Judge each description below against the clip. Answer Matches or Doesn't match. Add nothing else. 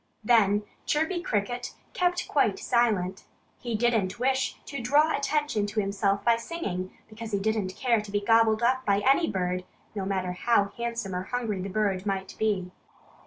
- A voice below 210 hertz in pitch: Doesn't match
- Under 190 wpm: Matches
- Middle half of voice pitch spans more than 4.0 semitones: Doesn't match